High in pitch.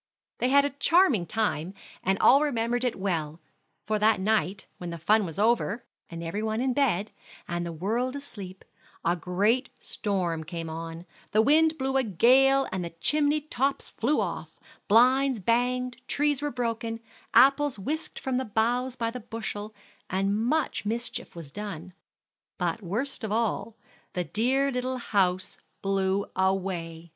Yes: high, 220 Hz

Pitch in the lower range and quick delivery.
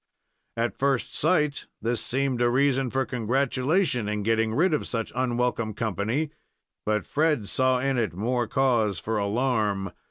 No: low, 120 Hz; average, 150 wpm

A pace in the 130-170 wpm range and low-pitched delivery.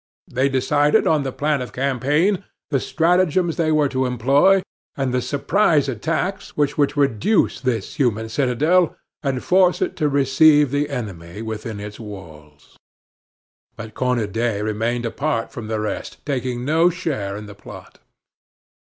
Yes: average, 150 wpm; low, 130 Hz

